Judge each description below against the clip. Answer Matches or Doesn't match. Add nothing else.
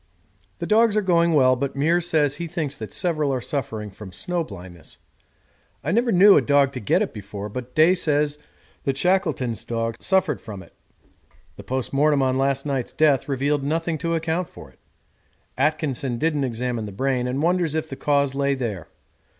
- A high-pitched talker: Doesn't match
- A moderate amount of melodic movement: Matches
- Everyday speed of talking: Matches